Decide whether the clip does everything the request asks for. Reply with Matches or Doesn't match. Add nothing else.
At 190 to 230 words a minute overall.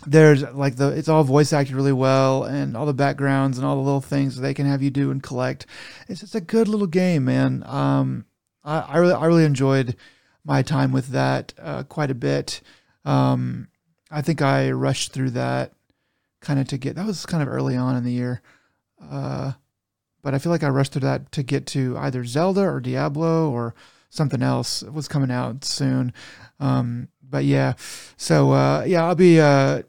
Matches